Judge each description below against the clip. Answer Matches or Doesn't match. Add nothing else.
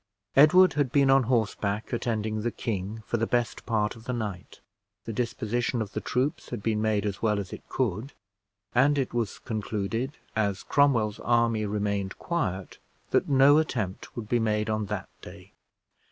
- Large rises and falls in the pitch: Doesn't match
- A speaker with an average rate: Matches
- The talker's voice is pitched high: Doesn't match